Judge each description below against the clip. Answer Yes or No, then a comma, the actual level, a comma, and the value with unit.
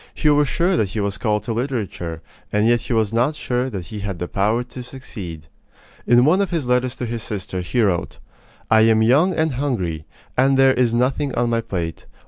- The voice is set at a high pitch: No, low, 120 Hz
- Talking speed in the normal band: No, fast, 215 wpm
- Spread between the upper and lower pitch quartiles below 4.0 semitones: No, average, 4.4 semitones